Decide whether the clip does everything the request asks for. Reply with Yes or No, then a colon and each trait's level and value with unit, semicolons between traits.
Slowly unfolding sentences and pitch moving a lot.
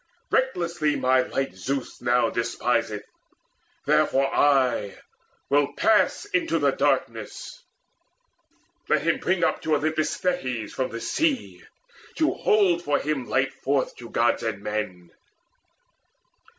Yes: slow, 120 wpm; wide, 6.4 semitones